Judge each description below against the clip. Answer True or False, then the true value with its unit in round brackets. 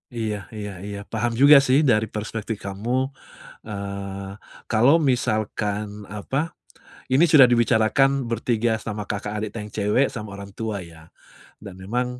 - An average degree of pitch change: True (3.4 semitones)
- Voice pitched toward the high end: False (110 Hz)